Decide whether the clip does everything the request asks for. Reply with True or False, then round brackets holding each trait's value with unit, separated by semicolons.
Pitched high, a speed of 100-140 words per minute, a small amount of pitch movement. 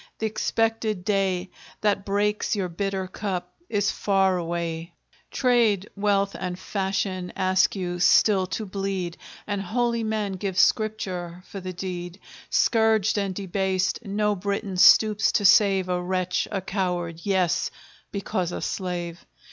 True (195 Hz; 135 wpm; 2.3 semitones)